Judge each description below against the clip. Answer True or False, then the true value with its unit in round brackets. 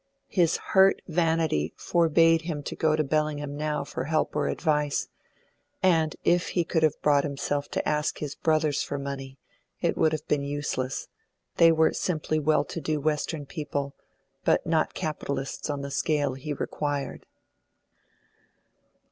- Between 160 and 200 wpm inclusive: False (150 wpm)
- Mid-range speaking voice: True (150 Hz)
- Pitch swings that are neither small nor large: False (2.0 semitones)